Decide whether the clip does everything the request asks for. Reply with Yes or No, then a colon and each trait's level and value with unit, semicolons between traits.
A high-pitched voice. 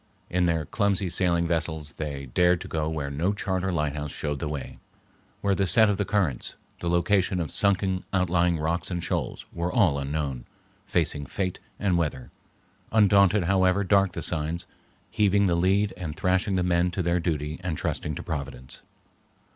No: very low, 85 Hz